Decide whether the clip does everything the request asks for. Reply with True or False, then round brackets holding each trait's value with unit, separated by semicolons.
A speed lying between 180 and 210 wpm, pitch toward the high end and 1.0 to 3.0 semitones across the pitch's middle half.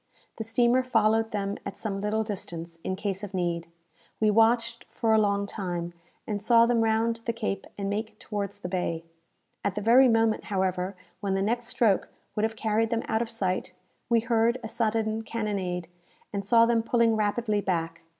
True (185 wpm; 215 Hz; 2.6 semitones)